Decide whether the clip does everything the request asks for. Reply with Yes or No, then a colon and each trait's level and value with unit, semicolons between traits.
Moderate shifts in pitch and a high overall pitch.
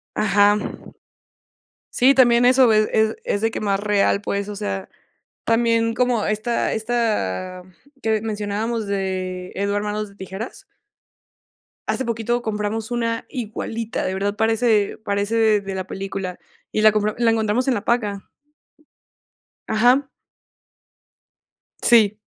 No: narrow, 2.2 semitones; high, 215 Hz